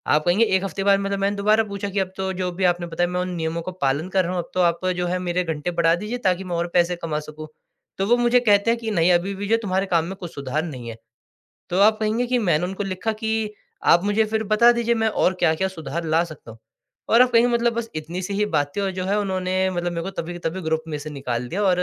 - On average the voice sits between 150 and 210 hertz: Yes, medium, 185 Hz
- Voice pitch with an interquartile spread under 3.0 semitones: No, average, 3.4 semitones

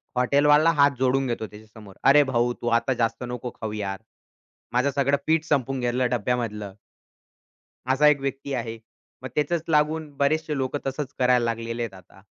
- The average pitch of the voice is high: No, low, 130 Hz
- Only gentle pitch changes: No, average, 3.6 semitones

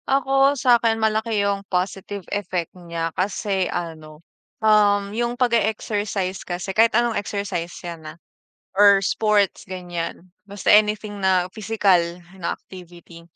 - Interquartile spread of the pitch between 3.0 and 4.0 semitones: Yes, average, 3.4 semitones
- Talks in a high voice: Yes, high, 200 Hz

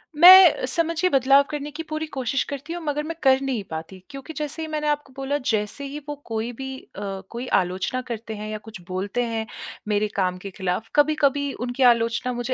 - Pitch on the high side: Yes, very high, 265 Hz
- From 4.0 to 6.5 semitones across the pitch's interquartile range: Yes, average, 5.1 semitones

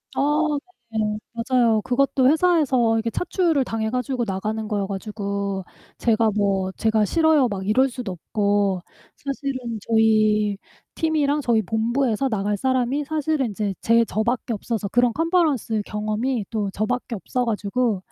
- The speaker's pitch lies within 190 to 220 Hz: No, high, 230 Hz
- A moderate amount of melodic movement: Yes, average, 4.0 semitones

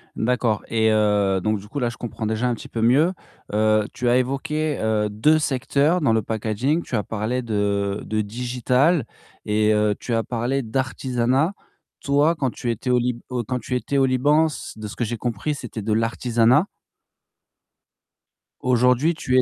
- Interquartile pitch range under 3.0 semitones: No, average, 3.4 semitones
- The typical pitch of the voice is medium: No, low, 120 Hz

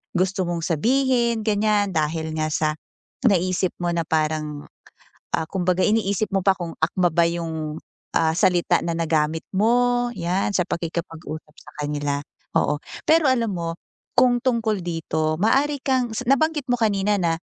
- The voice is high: No, medium, 180 Hz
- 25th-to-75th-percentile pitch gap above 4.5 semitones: Yes, wide, 5.6 semitones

